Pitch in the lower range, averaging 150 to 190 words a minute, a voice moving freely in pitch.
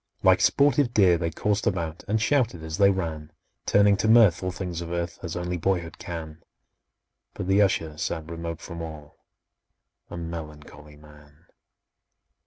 No: very low, 85 Hz; average, 155 wpm; average, 3.4 semitones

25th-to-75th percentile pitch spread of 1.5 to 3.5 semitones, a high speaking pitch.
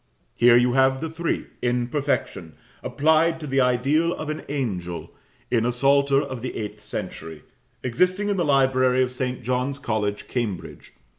No: average, 3.2 semitones; low, 130 Hz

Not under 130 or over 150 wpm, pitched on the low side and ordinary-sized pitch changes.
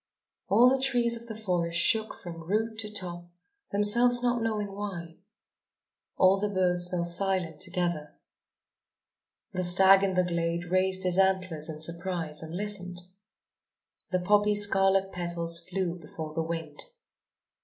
No: average, 140 wpm; medium, 185 Hz; average, 3.2 semitones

